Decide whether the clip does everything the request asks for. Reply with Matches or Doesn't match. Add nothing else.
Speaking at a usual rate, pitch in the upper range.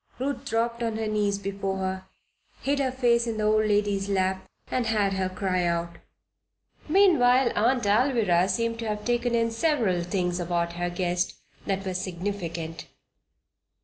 Matches